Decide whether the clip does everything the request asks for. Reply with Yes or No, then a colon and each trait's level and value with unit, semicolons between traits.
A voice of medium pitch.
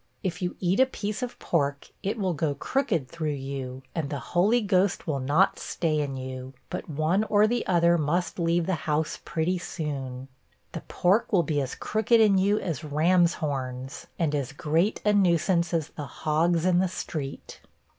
Yes: medium, 165 Hz